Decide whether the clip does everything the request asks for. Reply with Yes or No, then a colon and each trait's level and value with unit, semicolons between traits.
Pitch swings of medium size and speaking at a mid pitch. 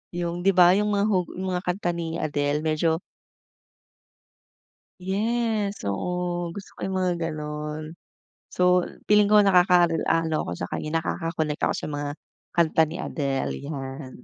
Yes: average, 3.2 semitones; medium, 170 Hz